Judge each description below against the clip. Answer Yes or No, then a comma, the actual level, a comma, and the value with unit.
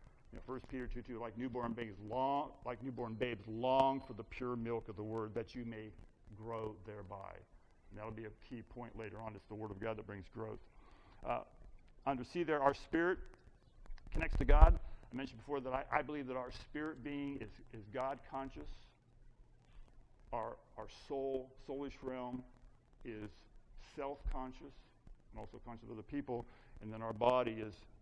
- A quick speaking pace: No, average, 180 wpm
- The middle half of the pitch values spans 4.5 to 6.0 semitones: No, average, 3.2 semitones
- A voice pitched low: Yes, low, 120 Hz